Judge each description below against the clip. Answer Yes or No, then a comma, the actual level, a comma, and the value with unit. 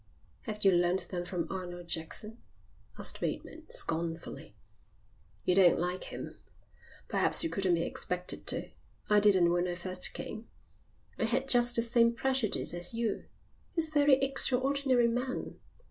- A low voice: No, high, 210 Hz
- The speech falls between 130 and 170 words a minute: Yes, average, 145 wpm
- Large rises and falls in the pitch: Yes, wide, 5.9 semitones